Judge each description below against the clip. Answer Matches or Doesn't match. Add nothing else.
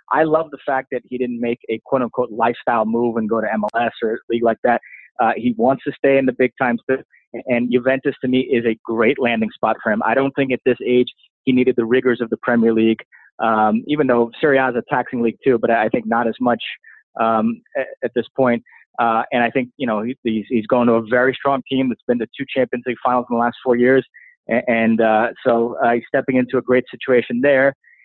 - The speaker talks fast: Matches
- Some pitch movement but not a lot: Doesn't match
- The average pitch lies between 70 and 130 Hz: Matches